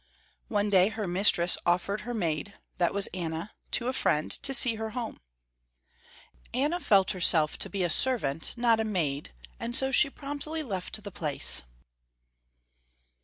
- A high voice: Yes, high, 205 Hz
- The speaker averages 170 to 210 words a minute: No, average, 155 wpm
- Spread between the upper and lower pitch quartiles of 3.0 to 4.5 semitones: No, wide, 5.6 semitones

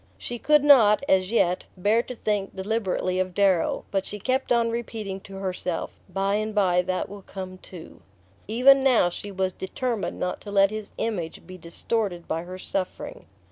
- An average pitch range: Yes, average, 3.4 semitones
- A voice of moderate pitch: No, high, 195 Hz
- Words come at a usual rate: Yes, average, 180 wpm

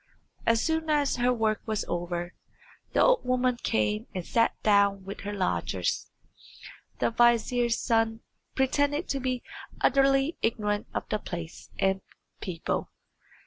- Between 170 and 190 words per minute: No, slow, 135 wpm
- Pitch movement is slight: No, average, 4.4 semitones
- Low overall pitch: No, high, 225 Hz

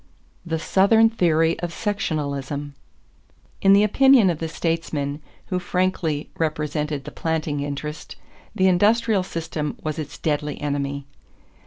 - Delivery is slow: Yes, slow, 125 wpm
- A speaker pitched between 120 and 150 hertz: No, medium, 160 Hz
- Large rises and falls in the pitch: No, average, 4.0 semitones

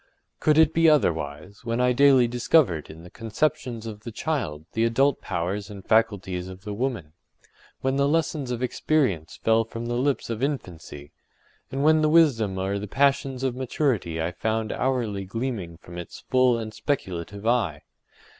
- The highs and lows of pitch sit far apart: Yes, wide, 5.8 semitones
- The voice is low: Yes, low, 115 Hz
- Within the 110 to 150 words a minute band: No, average, 165 wpm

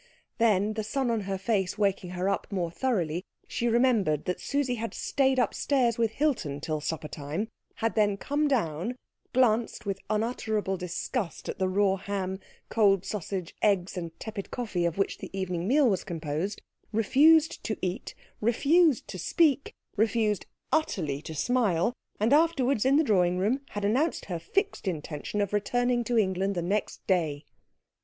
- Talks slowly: No, average, 165 wpm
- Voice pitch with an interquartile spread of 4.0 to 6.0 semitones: Yes, average, 5.1 semitones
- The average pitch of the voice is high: Yes, high, 205 Hz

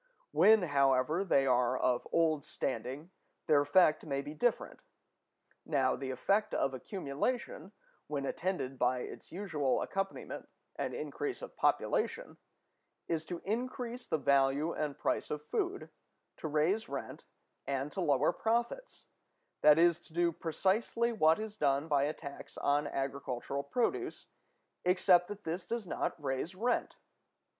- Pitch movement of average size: No, wide, 6.0 semitones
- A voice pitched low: No, medium, 155 Hz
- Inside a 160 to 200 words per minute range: No, average, 140 wpm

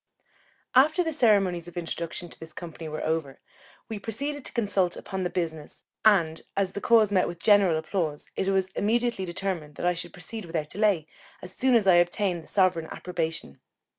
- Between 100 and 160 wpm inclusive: No, average, 185 wpm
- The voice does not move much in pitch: No, average, 3.9 semitones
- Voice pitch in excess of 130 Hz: Yes, medium, 185 Hz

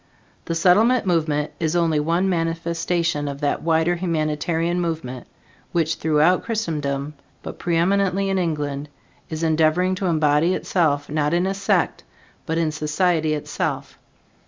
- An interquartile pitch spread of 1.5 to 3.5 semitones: Yes, narrow, 2.6 semitones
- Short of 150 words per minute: Yes, slow, 135 wpm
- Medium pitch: Yes, medium, 165 Hz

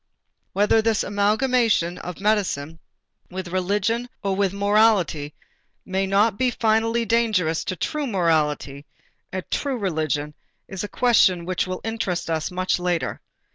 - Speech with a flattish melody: No, average, 4.1 semitones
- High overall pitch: Yes, high, 195 Hz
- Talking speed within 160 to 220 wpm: No, slow, 135 wpm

